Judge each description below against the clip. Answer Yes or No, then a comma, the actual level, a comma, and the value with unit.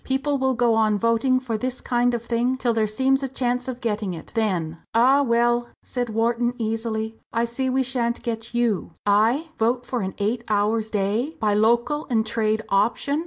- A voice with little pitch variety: Yes, narrow, 2.3 semitones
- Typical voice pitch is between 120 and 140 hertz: No, high, 235 Hz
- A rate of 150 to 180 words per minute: No, average, 190 wpm